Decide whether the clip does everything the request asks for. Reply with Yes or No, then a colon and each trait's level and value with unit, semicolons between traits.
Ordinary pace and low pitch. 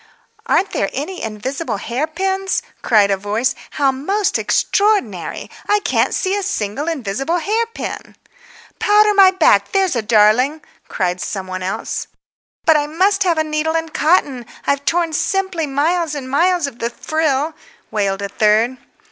No: average, 155 wpm; very high, 300 Hz